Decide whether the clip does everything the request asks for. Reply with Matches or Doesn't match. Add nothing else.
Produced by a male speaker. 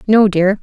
Doesn't match